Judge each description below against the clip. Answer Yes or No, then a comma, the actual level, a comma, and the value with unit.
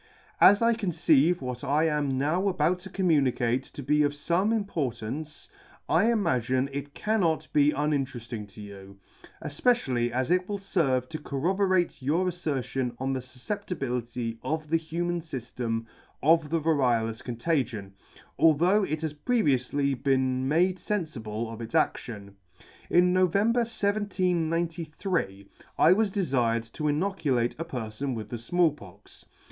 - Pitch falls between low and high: Yes, medium, 150 Hz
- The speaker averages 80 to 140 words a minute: Yes, slow, 135 wpm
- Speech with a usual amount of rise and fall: No, wide, 6.1 semitones